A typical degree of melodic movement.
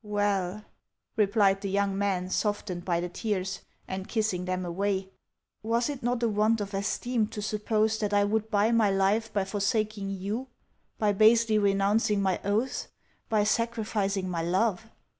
No: narrow, 2.2 semitones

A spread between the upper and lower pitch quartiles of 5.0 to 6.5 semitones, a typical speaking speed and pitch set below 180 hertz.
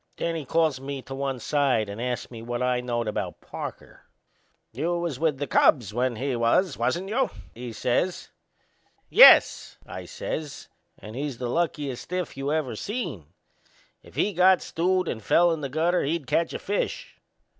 Yes: wide, 5.6 semitones; average, 175 wpm; medium, 140 Hz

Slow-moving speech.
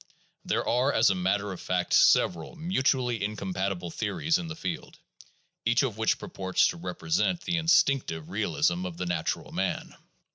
No: average, 160 wpm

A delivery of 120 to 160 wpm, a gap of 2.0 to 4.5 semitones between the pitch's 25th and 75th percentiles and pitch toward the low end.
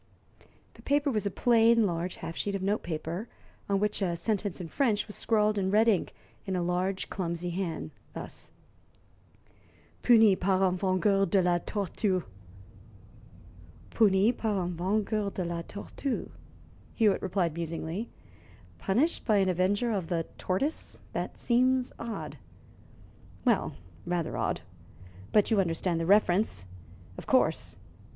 No: average, 140 wpm; average, 3.4 semitones; high, 195 Hz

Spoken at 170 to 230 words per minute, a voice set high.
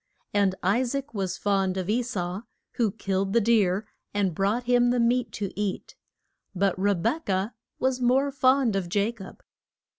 Yes: average, 175 wpm; high, 205 Hz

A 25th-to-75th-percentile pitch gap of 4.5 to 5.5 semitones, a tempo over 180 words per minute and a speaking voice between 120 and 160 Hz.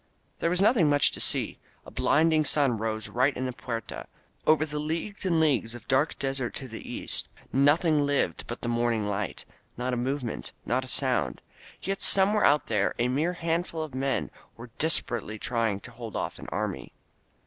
Yes: average, 4.9 semitones; average, 190 wpm; low, 135 Hz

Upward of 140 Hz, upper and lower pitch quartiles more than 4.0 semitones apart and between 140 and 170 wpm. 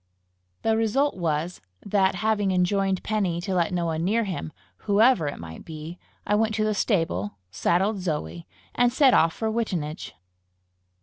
Yes: high, 190 Hz; average, 4.7 semitones; average, 160 wpm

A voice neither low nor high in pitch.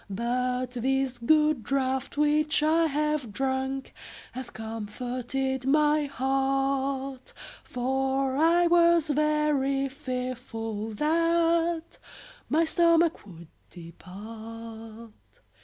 No: very high, 270 Hz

